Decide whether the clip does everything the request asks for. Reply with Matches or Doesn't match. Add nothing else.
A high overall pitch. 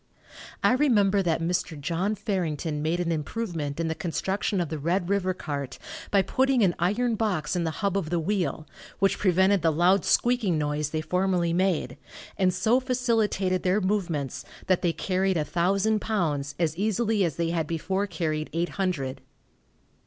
Doesn't match